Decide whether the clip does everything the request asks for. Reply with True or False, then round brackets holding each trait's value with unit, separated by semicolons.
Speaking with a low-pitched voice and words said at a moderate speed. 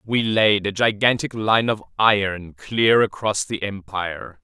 True (105 Hz; 150 wpm)